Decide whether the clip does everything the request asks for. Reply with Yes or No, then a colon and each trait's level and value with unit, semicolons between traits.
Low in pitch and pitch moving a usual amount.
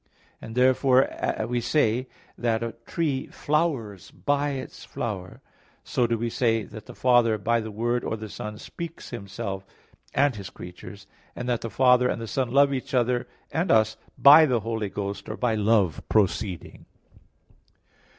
Yes: low, 115 Hz; average, 3.2 semitones